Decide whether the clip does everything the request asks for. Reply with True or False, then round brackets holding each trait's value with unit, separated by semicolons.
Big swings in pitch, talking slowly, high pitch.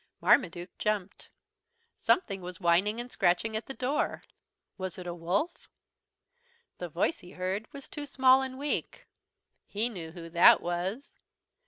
False (6.3 semitones; 145 wpm; 195 Hz)